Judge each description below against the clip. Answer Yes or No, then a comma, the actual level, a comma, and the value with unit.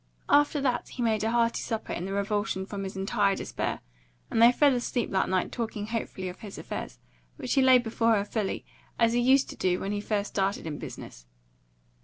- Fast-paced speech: Yes, fast, 210 wpm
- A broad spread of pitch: No, average, 3.5 semitones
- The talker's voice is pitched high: Yes, high, 220 Hz